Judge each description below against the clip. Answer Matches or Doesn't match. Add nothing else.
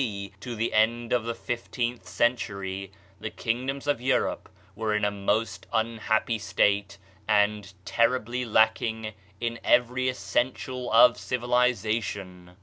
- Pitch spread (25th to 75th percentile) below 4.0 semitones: Matches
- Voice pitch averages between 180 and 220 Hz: Doesn't match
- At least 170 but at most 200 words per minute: Doesn't match